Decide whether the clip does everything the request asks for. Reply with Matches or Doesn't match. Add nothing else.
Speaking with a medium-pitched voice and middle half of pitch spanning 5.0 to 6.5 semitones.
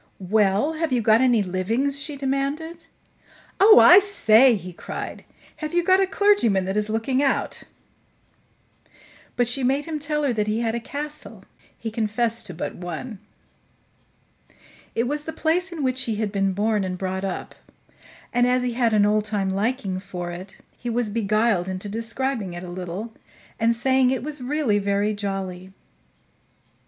Doesn't match